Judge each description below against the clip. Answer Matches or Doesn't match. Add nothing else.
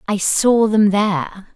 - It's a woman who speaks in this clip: Matches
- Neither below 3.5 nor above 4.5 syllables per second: Matches